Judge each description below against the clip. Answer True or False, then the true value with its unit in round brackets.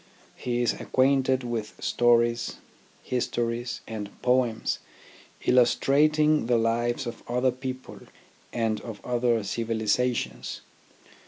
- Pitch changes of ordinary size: False (1.8 semitones)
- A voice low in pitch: True (120 Hz)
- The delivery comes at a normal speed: False (95 wpm)